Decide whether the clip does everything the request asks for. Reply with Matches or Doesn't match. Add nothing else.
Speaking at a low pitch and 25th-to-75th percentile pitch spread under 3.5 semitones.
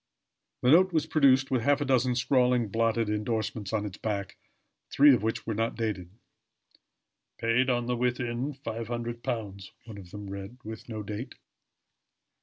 Matches